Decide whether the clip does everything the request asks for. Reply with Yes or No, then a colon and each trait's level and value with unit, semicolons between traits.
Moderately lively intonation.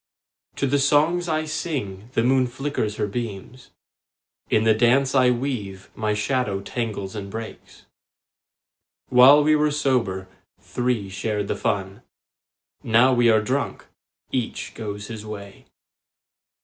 Yes: average, 4.4 semitones